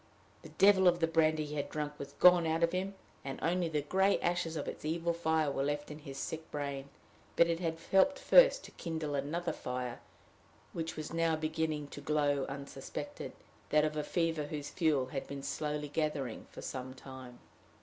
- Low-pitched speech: No, medium, 155 Hz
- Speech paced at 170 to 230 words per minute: Yes, average, 190 wpm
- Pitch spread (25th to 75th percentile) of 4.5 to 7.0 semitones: No, average, 2.7 semitones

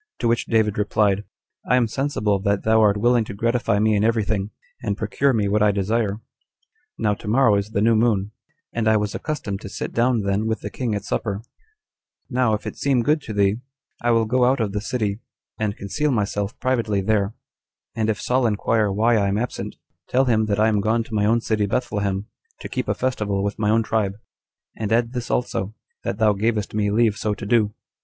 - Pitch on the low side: Yes, low, 110 Hz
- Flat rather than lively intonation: Yes, narrow, 2.3 semitones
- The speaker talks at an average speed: No, fast, 215 wpm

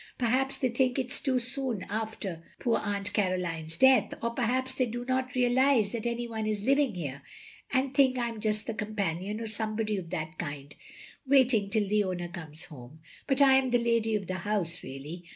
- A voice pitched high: Yes, high, 220 Hz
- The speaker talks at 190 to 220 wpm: Yes, average, 200 wpm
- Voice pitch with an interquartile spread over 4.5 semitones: Yes, wide, 5.4 semitones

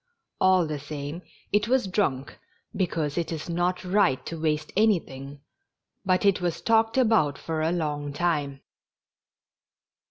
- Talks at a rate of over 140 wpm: No, slow, 135 wpm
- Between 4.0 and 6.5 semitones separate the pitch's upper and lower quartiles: Yes, average, 4.3 semitones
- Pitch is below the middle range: No, medium, 165 Hz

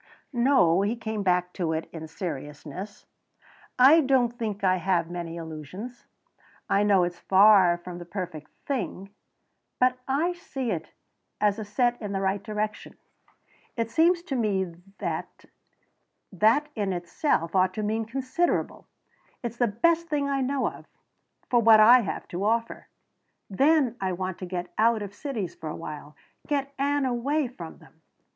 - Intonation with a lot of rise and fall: Yes, wide, 5.9 semitones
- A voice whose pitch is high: Yes, high, 210 Hz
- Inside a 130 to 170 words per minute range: Yes, average, 155 wpm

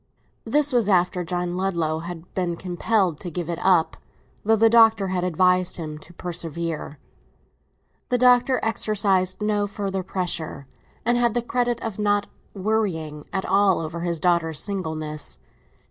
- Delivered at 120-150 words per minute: Yes, average, 145 wpm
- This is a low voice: No, medium, 185 Hz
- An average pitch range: Yes, average, 3.9 semitones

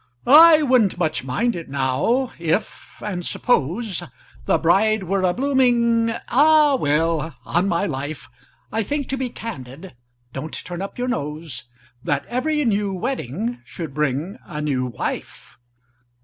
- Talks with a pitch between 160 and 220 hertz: Yes, medium, 185 Hz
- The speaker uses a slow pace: Yes, slow, 120 wpm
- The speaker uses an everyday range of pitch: No, wide, 8.4 semitones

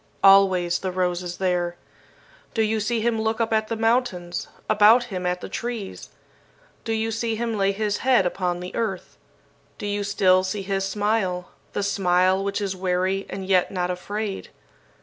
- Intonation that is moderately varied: Yes, average, 3.1 semitones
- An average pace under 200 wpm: Yes, average, 175 wpm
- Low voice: No, high, 195 Hz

